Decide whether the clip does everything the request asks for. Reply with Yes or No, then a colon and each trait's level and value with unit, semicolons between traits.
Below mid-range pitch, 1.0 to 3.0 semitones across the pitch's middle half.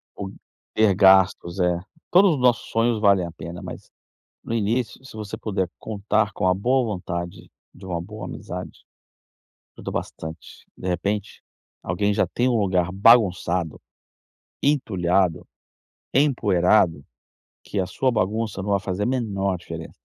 No: low, 100 Hz; average, 3.7 semitones